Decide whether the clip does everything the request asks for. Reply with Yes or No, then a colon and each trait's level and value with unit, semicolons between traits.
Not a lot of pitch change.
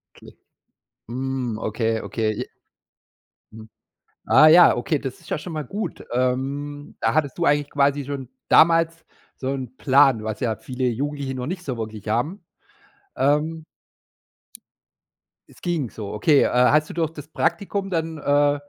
No: average, 3.9 semitones